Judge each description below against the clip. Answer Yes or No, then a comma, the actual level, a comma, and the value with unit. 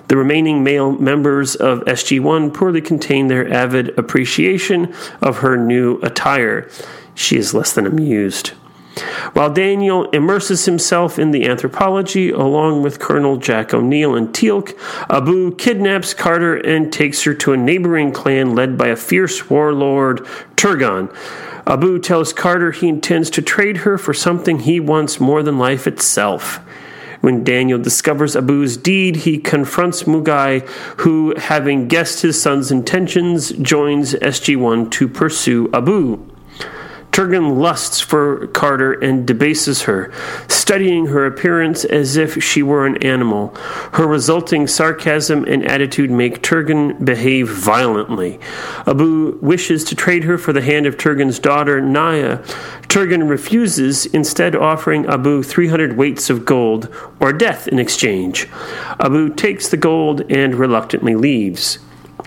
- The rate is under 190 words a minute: Yes, average, 140 wpm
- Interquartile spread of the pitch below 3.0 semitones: No, average, 3.7 semitones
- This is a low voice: No, medium, 150 Hz